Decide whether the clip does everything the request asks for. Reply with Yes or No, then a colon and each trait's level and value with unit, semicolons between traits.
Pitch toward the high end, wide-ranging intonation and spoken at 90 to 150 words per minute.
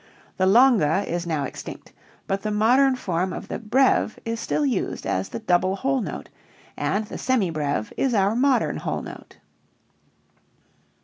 No: high, 210 Hz; wide, 5.9 semitones; average, 160 wpm